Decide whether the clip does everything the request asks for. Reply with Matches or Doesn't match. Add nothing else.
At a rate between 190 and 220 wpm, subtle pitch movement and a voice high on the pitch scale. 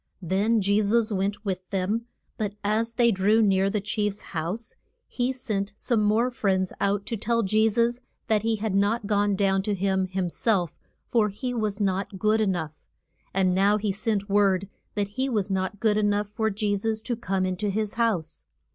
Matches